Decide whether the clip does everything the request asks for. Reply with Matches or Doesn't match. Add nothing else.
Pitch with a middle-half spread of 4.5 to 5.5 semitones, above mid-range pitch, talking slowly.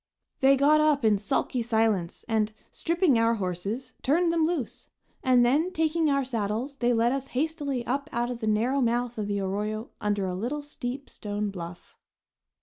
Doesn't match